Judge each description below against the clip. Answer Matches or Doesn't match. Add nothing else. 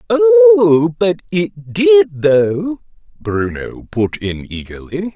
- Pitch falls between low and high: Matches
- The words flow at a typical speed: Doesn't match